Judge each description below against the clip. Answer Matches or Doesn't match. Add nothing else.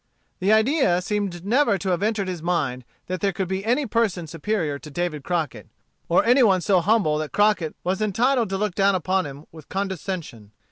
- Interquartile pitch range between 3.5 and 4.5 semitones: Matches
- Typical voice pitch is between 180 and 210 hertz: Matches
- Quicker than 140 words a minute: Matches